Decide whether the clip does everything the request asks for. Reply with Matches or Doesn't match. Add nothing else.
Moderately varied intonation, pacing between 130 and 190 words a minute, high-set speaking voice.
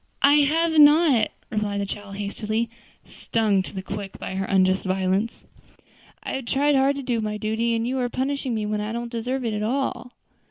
Doesn't match